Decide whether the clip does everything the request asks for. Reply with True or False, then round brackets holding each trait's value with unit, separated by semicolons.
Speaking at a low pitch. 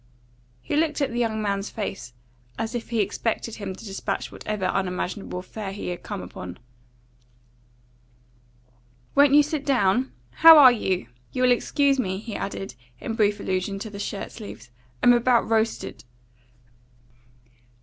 False (220 Hz)